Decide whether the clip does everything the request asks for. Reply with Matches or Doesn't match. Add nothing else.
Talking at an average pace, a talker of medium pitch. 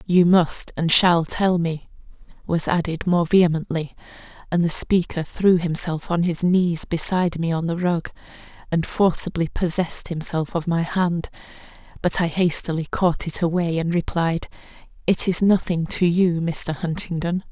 Matches